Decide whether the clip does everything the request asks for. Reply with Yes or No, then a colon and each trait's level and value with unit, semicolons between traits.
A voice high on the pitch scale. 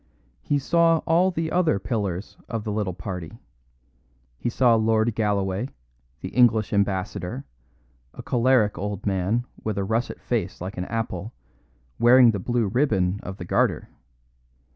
No: low, 110 Hz